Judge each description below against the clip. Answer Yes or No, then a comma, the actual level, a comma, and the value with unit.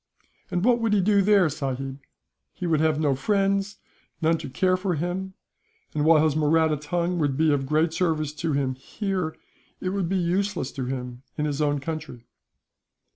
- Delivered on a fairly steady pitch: No, average, 4.2 semitones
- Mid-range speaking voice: Yes, medium, 160 Hz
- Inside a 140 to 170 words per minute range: No, average, 185 wpm